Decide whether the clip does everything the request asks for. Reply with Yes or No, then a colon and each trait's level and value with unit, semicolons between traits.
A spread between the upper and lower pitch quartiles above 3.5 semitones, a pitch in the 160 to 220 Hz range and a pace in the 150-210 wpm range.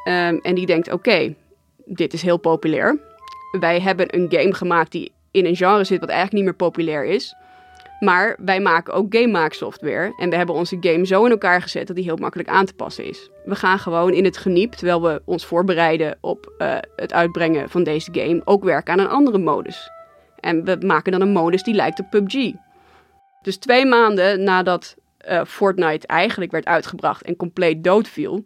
No: average, 2.8 semitones; medium, 185 Hz; fast, 200 wpm